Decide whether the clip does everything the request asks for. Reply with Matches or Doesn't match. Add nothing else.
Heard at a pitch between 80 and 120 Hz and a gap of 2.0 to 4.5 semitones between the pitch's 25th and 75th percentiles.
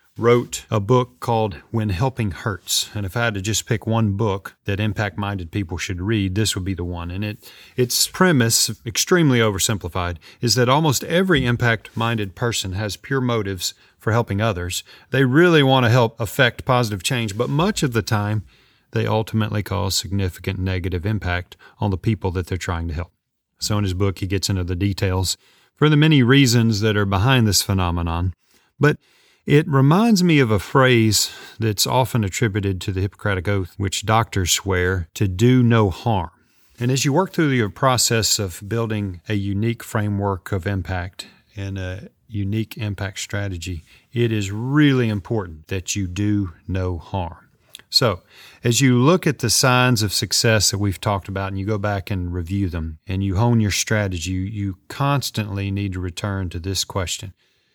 Matches